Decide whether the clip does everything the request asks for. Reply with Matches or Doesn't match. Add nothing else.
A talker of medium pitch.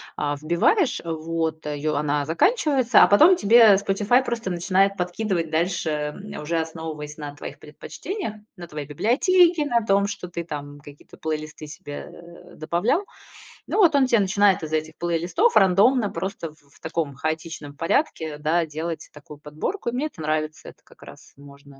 Matches